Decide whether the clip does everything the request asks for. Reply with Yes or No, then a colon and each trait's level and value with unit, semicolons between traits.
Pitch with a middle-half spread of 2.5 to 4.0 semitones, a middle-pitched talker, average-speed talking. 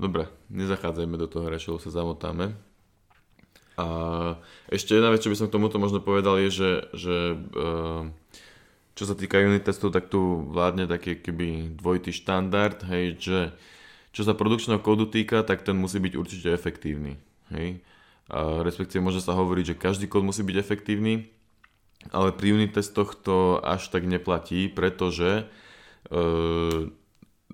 No: average, 2.9 semitones; very low, 95 Hz; average, 150 wpm